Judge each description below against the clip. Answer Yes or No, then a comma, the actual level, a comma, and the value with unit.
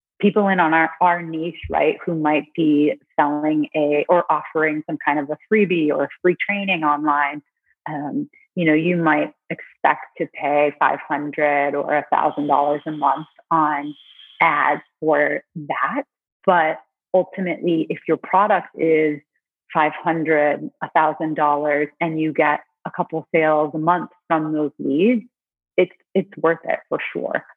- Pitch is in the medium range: Yes, medium, 155 Hz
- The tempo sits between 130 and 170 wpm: Yes, average, 155 wpm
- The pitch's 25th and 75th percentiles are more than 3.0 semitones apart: No, average, 2.7 semitones